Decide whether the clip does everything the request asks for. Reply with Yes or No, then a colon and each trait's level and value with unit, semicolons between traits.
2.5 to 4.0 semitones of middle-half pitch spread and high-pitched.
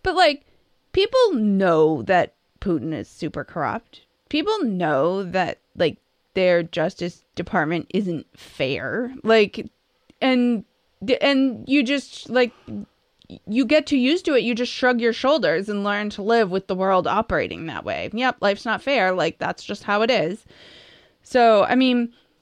No: average, 5.3 semitones; high, 230 Hz